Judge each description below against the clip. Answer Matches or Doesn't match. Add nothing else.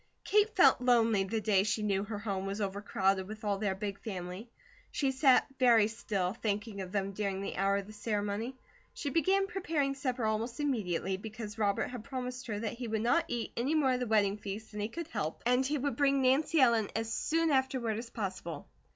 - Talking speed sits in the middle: Doesn't match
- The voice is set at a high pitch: Matches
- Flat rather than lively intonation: Doesn't match